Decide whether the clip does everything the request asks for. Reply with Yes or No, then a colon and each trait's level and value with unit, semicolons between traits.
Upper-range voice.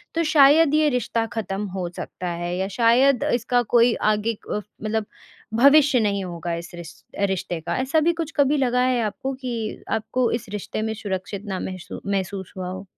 Yes: high, 220 Hz